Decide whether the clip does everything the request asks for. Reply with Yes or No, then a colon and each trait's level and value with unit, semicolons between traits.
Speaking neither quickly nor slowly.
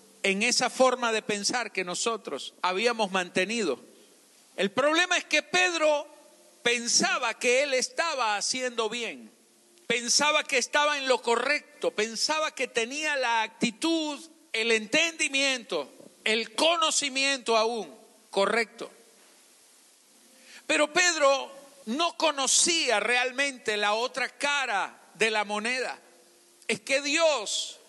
No: slow, 110 wpm